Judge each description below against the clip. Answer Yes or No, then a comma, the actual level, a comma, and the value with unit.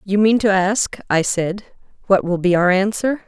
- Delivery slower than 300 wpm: Yes, average, 200 wpm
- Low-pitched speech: No, high, 200 Hz